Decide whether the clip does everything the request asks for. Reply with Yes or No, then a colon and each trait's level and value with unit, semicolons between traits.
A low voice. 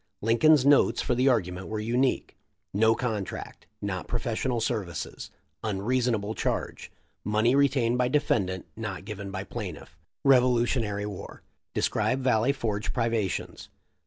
Yes: low, 115 Hz